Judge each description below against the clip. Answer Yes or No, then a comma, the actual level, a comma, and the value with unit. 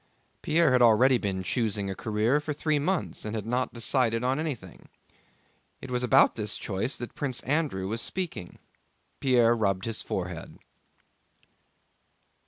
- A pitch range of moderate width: Yes, average, 4.2 semitones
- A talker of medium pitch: No, low, 120 Hz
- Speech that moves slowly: No, average, 145 wpm